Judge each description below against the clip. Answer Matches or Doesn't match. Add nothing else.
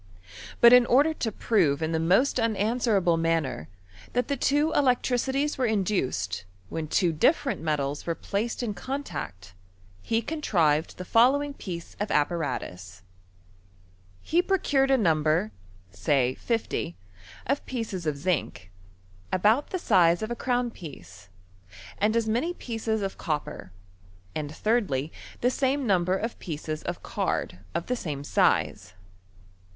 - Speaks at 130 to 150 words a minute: Matches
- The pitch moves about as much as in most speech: Doesn't match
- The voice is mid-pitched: Doesn't match